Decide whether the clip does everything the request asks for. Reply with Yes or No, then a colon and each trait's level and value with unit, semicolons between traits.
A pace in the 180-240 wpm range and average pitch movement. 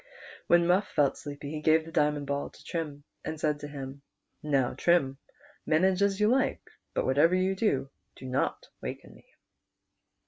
No: average, 170 wpm; average, 3.8 semitones